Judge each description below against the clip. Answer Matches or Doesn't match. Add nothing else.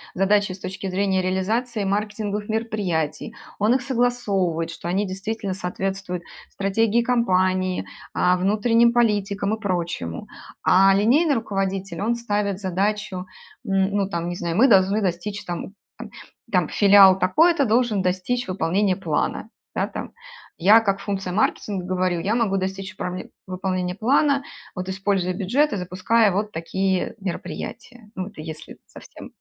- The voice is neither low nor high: Doesn't match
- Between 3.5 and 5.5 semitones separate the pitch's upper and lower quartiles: Doesn't match